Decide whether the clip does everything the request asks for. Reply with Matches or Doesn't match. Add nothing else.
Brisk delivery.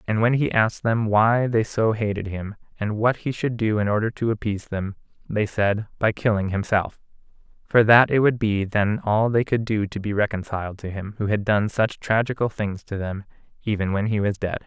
Matches